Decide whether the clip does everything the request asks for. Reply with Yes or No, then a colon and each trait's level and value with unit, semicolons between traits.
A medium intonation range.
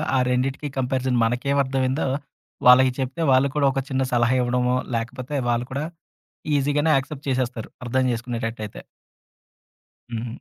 No: narrow, 1.9 semitones